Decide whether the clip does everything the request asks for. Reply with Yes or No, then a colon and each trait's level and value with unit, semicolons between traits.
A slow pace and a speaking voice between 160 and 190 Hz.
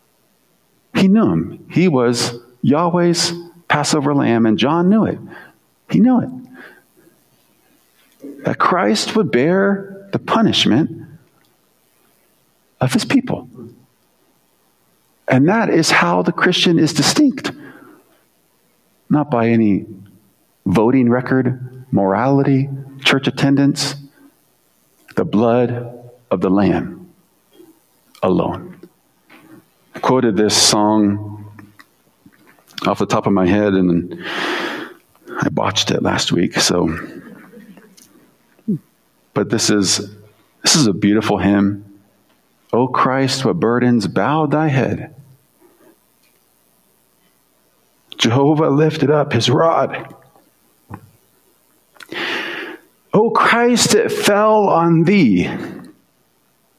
No: slow, 95 wpm; low, 135 Hz